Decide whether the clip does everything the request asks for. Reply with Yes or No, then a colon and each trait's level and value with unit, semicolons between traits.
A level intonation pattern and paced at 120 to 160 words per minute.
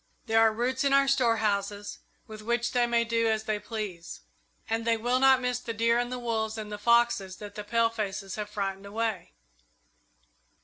No: narrow, 2.2 semitones; average, 185 wpm